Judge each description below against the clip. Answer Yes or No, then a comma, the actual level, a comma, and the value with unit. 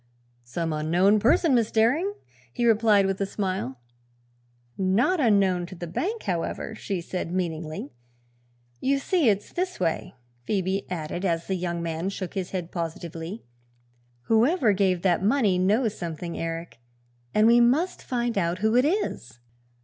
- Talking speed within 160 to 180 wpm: No, average, 150 wpm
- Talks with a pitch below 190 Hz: No, high, 195 Hz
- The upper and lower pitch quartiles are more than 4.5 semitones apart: Yes, average, 5.1 semitones